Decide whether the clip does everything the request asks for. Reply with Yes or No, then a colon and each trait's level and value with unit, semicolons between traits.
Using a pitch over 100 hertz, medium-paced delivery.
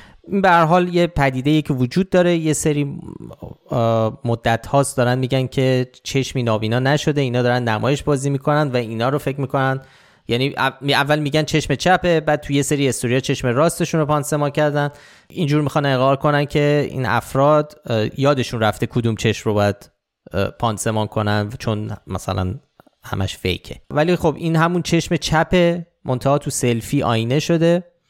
No: medium, 140 Hz; fast, 160 wpm